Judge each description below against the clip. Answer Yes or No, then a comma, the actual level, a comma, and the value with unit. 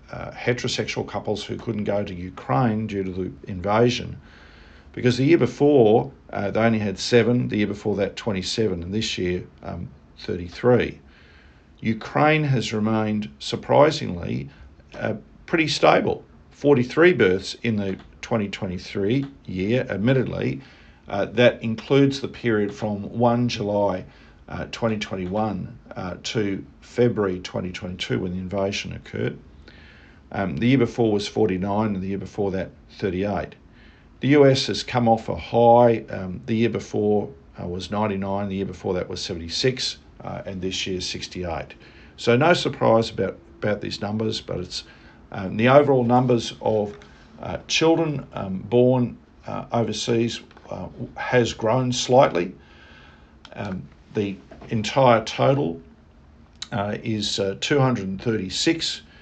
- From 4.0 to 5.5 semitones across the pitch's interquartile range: Yes, average, 4.5 semitones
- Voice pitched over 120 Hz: No, low, 105 Hz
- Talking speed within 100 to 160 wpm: Yes, slow, 135 wpm